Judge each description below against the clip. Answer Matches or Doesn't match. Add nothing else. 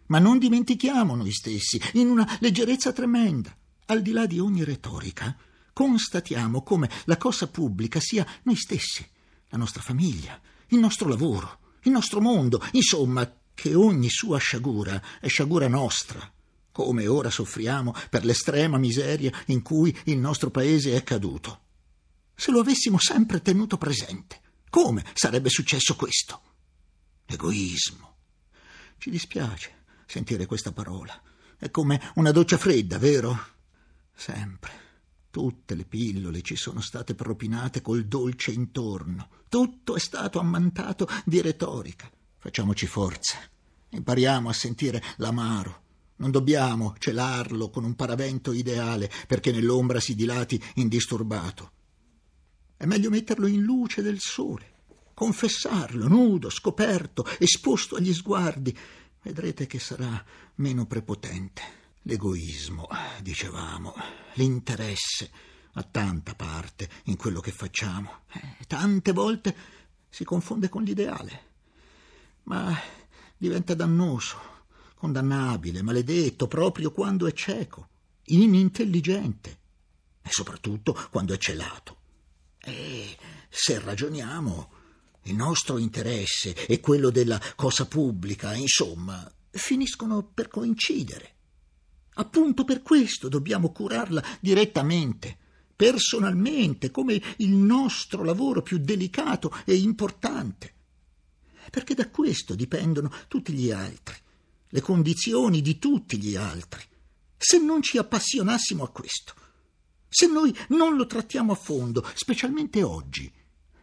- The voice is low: Matches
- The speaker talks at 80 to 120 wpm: Matches